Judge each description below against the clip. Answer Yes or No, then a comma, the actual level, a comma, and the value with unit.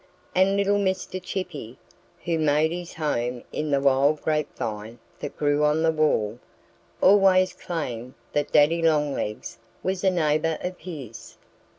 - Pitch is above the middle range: No, medium, 155 Hz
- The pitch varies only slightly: No, average, 4.3 semitones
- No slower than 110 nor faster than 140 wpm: Yes, slow, 135 wpm